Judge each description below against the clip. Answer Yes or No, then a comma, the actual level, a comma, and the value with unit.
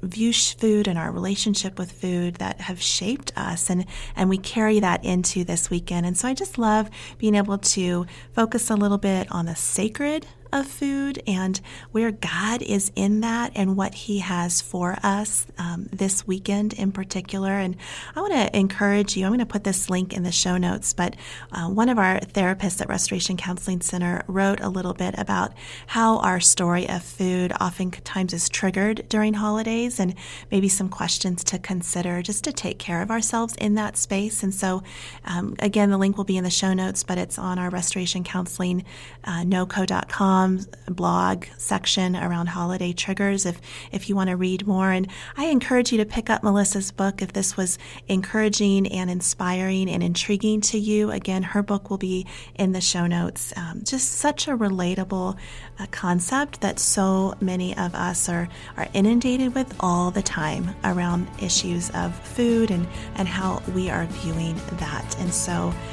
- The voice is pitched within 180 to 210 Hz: Yes, high, 190 Hz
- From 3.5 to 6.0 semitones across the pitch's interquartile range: No, narrow, 2.5 semitones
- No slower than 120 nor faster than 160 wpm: No, average, 185 wpm